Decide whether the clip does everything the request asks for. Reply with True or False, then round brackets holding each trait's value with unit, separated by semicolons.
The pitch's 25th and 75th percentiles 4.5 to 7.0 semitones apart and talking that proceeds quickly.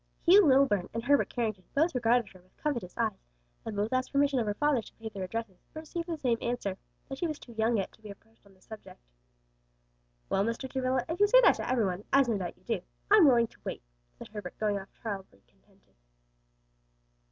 True (5.0 semitones; 220 wpm)